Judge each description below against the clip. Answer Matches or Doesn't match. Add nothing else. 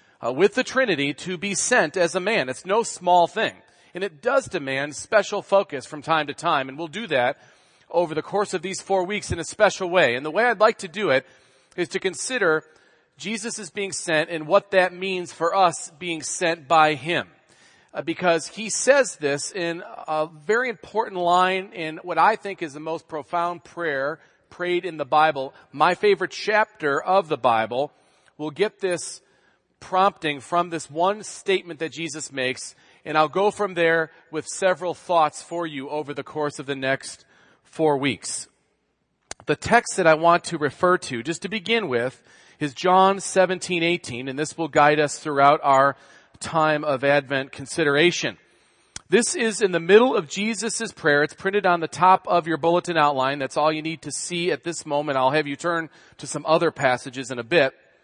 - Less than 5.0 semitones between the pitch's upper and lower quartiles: Matches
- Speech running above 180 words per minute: Matches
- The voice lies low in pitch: Doesn't match